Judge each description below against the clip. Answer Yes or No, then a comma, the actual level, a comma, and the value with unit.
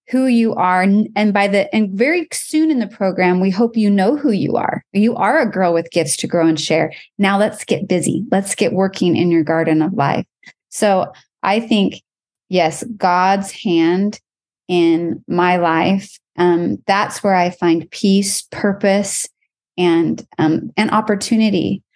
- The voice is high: Yes, high, 195 Hz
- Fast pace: No, average, 165 wpm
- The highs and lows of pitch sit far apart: No, average, 3.4 semitones